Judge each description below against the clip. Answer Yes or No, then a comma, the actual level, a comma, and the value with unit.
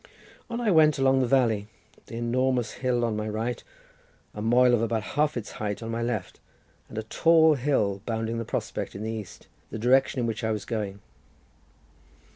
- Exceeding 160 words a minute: Yes, average, 190 wpm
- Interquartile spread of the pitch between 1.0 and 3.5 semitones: Yes, average, 3.0 semitones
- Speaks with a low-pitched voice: Yes, low, 115 Hz